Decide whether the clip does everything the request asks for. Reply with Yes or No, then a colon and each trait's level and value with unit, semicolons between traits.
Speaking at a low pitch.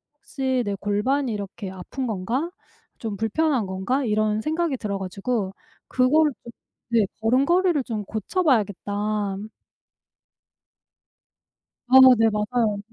No: high, 225 Hz